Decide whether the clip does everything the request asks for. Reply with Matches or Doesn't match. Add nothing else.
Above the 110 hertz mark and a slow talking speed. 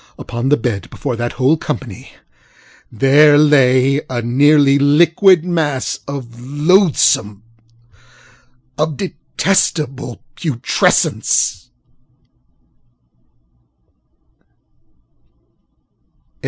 Matches